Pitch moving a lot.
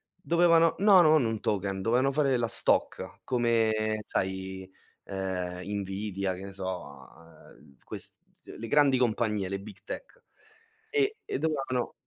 Yes: wide, 6.2 semitones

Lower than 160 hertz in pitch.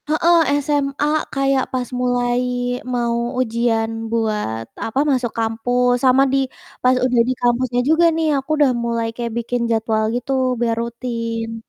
No: high, 245 Hz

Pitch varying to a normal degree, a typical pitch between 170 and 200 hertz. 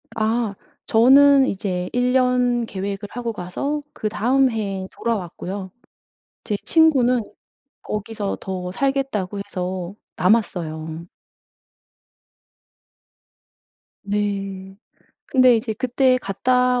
No: average, 4.7 semitones; high, 215 Hz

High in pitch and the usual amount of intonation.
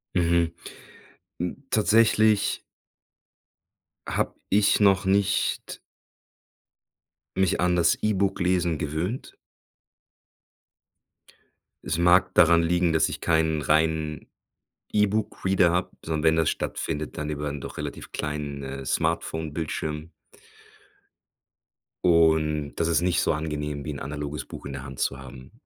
No: very low, 80 Hz; average, 3.2 semitones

